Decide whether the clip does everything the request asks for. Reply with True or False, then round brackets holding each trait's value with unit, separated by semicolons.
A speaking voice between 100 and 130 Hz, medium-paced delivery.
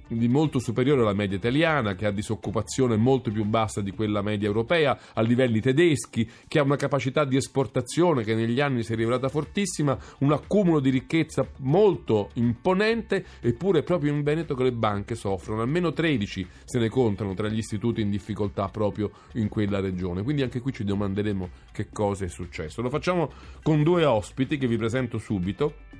False (120 Hz; 180 wpm)